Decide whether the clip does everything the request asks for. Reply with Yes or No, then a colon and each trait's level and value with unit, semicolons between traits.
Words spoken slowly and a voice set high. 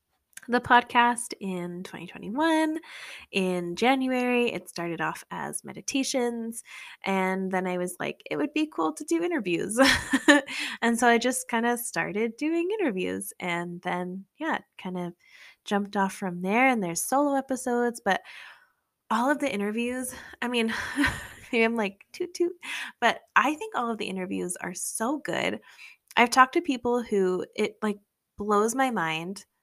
No: average, 155 wpm; high, 235 Hz